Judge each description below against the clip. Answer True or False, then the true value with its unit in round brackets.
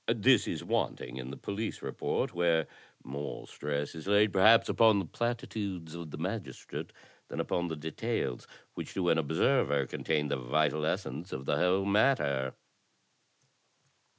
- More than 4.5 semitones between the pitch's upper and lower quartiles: True (5.6 semitones)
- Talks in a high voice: False (80 Hz)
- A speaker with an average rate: True (150 wpm)